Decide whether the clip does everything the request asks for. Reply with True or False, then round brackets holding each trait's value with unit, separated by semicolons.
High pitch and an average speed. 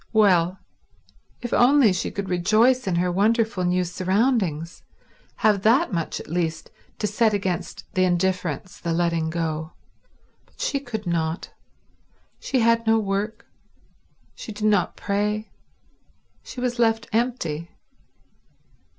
False (200 Hz; 125 wpm)